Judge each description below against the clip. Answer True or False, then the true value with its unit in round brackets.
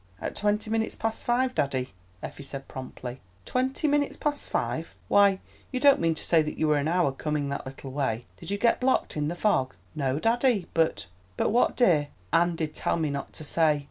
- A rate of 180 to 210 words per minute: True (205 wpm)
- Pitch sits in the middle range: True (165 Hz)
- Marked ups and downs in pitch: True (8.0 semitones)